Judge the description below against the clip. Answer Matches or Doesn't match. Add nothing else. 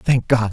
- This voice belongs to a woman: Doesn't match